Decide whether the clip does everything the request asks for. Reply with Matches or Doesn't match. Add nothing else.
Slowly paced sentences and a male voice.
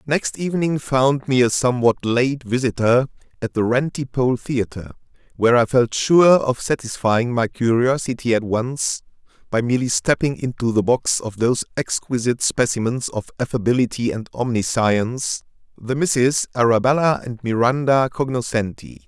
Matches